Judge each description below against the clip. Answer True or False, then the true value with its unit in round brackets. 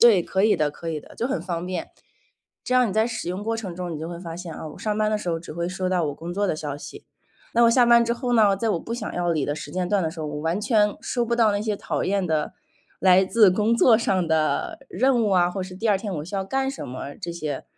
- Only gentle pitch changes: False (4.9 semitones)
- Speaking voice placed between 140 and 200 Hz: True (190 Hz)